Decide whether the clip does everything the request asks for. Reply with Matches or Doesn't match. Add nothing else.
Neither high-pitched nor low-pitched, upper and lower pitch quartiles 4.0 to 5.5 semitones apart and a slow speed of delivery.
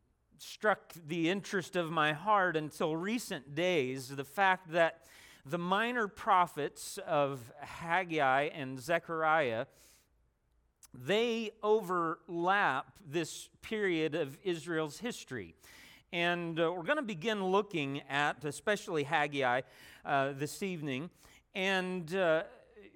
Matches